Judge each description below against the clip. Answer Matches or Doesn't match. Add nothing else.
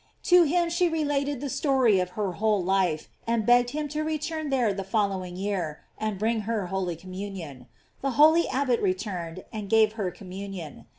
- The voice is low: Doesn't match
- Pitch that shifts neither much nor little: Doesn't match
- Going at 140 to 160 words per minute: Doesn't match